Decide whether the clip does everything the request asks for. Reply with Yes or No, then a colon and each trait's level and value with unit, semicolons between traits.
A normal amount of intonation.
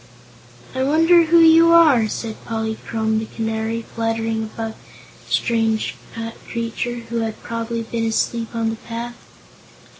No: narrow, 1.4 semitones